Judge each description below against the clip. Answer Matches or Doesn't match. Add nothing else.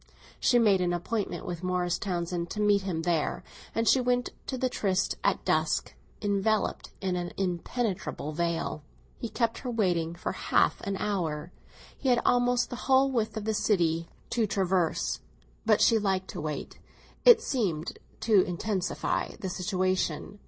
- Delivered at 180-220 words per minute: Doesn't match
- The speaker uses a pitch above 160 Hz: Matches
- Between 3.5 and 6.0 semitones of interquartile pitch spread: Matches